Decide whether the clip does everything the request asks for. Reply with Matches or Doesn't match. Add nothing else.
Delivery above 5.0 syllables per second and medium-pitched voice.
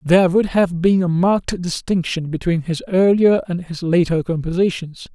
Doesn't match